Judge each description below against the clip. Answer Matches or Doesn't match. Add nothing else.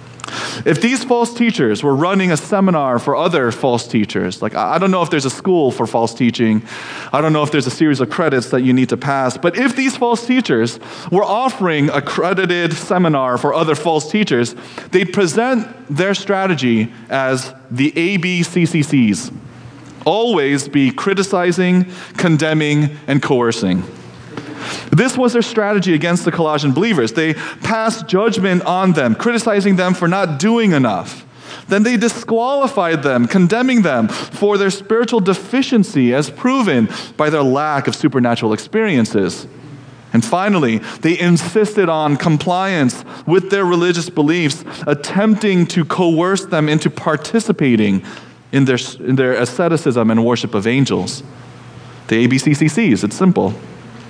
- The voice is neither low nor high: Matches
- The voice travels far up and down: Matches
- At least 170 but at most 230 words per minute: Doesn't match